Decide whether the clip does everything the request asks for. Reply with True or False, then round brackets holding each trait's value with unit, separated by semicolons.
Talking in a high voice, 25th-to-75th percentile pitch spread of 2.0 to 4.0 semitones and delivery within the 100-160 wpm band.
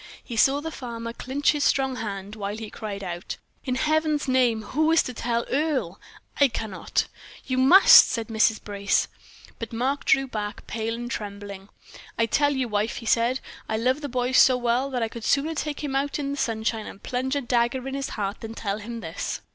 False (240 Hz; 3.7 semitones; 205 wpm)